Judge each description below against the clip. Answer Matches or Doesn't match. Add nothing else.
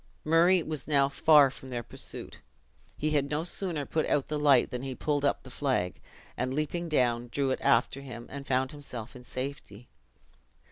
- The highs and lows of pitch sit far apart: Doesn't match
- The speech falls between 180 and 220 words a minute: Matches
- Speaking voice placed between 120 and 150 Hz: Matches